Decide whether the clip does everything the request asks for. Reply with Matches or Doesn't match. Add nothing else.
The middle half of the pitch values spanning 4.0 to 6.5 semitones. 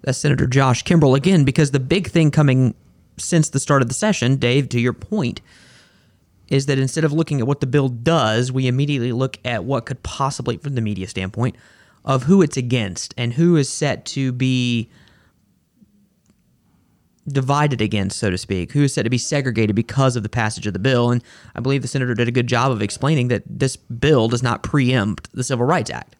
Doesn't match